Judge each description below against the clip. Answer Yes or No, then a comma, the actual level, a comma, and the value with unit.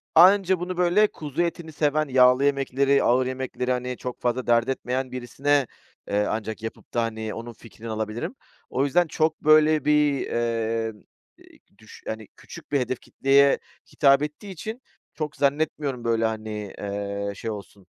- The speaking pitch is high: No, low, 130 Hz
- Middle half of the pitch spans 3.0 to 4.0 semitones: No, average, 4.7 semitones